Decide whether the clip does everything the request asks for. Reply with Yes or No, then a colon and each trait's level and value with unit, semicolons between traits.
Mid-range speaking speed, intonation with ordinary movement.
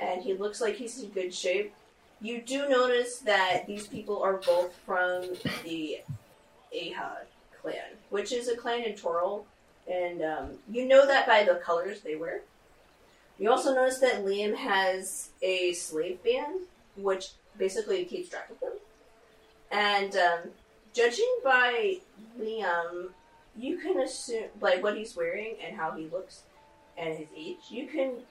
No: average, 155 wpm; wide, 6.4 semitones